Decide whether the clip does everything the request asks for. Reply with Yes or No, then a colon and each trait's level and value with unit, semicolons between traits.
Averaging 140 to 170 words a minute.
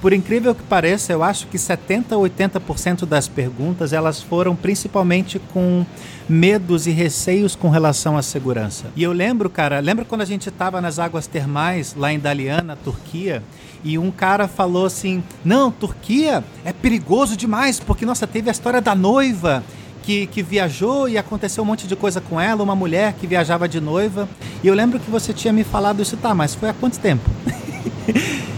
No: fast, 185 wpm